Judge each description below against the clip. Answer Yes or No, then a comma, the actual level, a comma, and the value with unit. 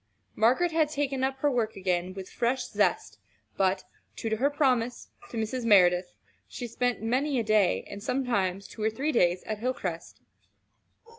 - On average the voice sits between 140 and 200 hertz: No, high, 230 Hz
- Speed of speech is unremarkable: Yes, average, 165 wpm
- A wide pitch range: No, average, 5.0 semitones